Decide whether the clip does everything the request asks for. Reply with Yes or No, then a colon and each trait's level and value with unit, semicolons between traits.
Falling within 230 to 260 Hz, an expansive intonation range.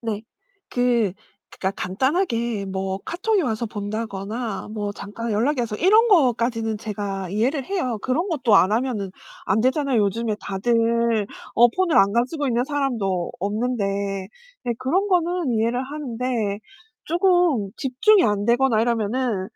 No: high, 235 Hz; average, 4.4 semitones